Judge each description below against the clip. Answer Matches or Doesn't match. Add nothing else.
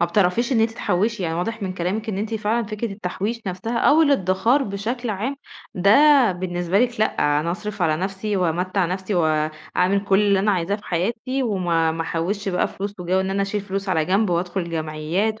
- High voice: Matches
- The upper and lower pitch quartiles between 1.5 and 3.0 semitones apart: Doesn't match